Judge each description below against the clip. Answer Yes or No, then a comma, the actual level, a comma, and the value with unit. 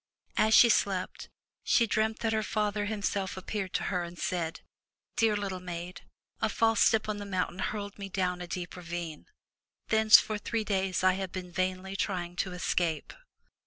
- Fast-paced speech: No, average, 175 wpm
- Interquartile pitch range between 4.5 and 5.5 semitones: No, average, 2.9 semitones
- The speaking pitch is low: No, high, 190 Hz